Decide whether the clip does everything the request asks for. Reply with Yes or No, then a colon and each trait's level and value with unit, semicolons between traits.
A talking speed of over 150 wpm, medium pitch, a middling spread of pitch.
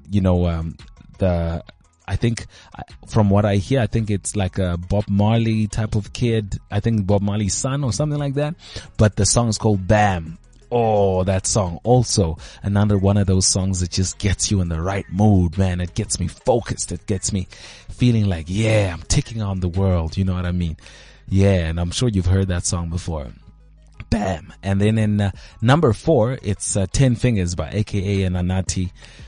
No: average, 200 wpm; low, 100 Hz; average, 3.1 semitones